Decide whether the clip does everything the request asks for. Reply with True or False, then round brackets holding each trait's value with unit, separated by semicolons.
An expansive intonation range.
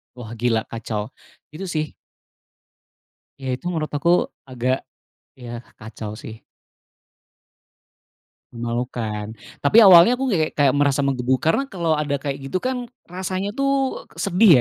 True (7.2 semitones)